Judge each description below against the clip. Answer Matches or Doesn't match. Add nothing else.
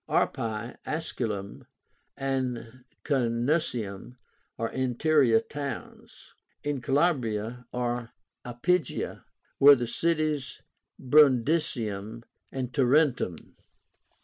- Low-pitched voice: Matches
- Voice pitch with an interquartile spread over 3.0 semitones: Matches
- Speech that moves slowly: Matches